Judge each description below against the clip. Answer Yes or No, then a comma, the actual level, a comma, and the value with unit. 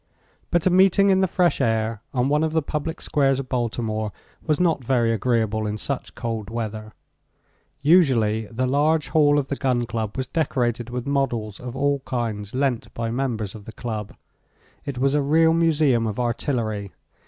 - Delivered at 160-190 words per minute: Yes, average, 175 wpm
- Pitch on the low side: Yes, low, 125 Hz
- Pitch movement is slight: No, average, 4.5 semitones